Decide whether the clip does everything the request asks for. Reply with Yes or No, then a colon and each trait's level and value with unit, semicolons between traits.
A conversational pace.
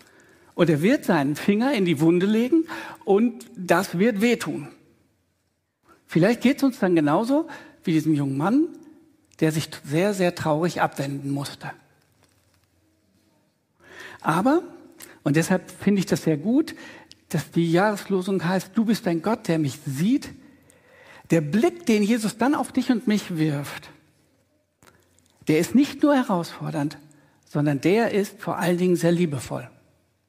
Yes: average, 145 wpm